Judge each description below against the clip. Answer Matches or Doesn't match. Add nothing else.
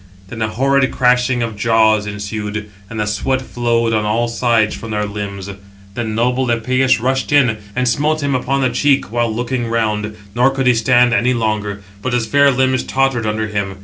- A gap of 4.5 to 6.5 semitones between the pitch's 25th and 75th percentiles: Doesn't match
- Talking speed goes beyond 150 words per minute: Matches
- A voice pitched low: Matches